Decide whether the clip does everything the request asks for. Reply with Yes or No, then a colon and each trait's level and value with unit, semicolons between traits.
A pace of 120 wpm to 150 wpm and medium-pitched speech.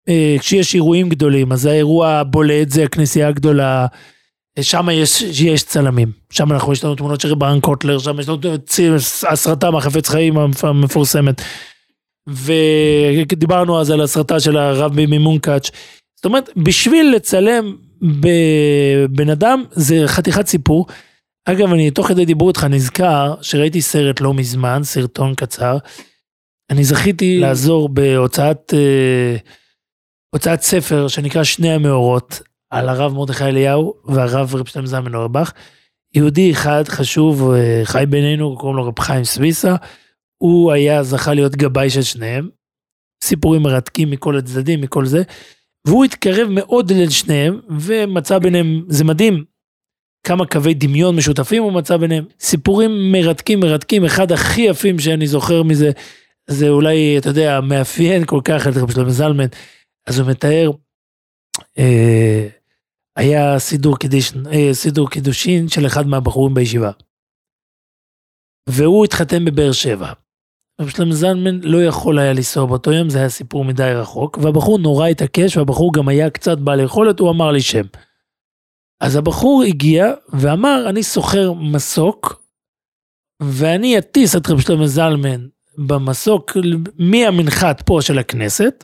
Yes: average, 135 wpm; medium, 150 Hz